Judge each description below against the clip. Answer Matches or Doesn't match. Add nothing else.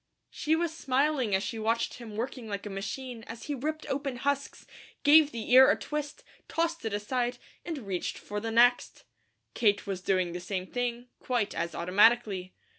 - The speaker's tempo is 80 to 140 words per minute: Doesn't match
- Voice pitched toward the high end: Matches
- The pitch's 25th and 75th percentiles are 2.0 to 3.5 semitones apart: Doesn't match